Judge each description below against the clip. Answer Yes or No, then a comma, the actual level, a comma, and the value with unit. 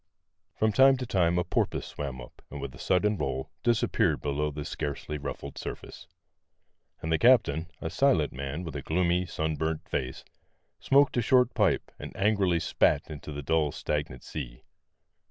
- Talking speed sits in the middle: Yes, average, 165 wpm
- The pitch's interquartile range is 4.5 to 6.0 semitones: Yes, average, 5.3 semitones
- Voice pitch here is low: Yes, very low, 80 Hz